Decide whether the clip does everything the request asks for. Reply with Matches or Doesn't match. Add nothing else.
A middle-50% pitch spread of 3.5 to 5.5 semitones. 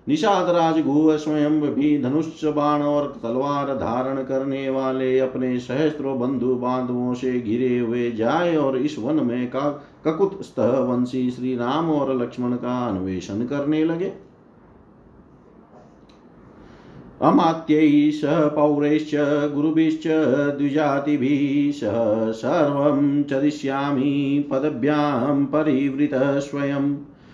Doesn't match